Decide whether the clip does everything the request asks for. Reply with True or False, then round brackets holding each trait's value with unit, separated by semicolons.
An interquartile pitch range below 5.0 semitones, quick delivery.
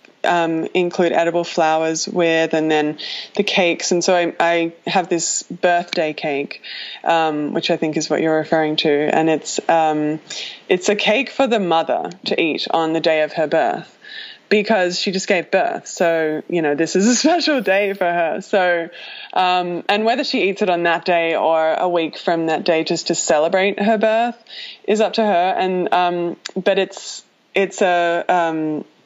False (3.3 semitones; 185 wpm)